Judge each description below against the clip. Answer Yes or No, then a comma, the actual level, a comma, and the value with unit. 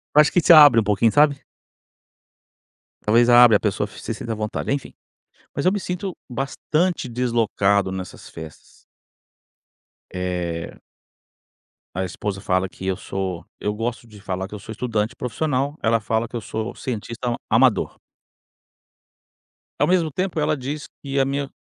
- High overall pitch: No, low, 115 Hz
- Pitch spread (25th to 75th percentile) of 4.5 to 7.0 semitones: Yes, wide, 5.4 semitones